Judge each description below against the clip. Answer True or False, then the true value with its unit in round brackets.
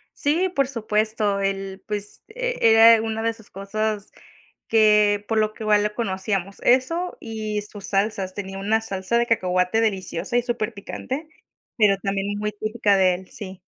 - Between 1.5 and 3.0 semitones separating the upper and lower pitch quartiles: True (2.4 semitones)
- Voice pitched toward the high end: True (210 Hz)